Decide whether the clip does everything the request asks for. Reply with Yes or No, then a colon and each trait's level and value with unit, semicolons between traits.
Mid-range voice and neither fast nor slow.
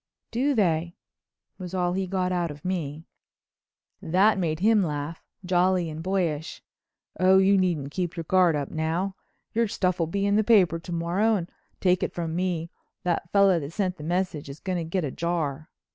Yes: medium, 180 Hz; average, 185 wpm